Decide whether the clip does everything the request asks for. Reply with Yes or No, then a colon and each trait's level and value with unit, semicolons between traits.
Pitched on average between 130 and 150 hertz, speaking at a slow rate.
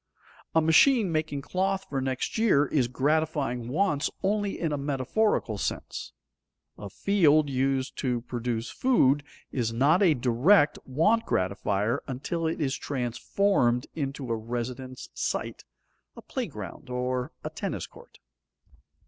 Yes: medium, 140 Hz; slow, 130 wpm